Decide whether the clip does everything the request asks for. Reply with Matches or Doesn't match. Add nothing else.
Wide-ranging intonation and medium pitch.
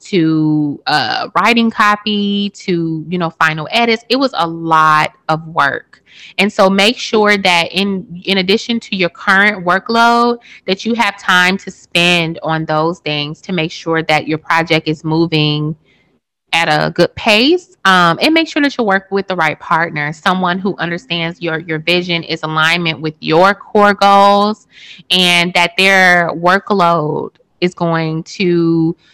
Doesn't match